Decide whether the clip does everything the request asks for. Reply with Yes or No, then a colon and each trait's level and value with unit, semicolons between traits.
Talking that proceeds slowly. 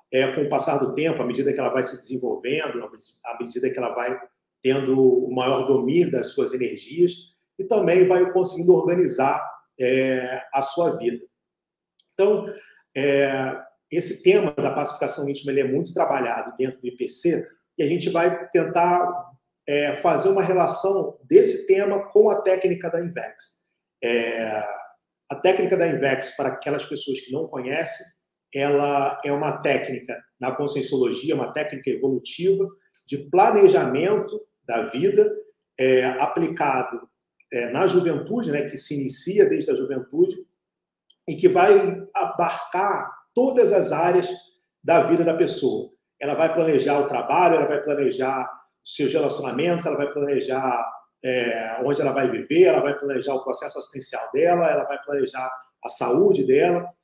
No: average, 150 wpm